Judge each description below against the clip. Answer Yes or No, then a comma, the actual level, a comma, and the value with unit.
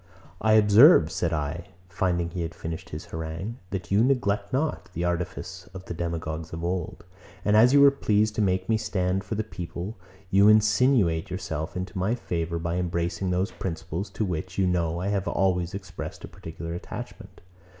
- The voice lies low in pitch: Yes, very low, 90 Hz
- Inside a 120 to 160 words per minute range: No, average, 185 wpm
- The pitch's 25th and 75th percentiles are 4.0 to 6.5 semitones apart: No, average, 3.6 semitones